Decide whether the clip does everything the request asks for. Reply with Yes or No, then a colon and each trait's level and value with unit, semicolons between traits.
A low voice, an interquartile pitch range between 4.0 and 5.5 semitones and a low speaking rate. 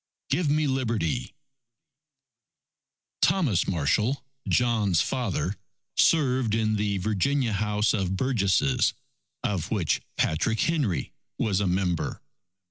Yes: low, 110 Hz; average, 5.1 semitones; slow, 100 wpm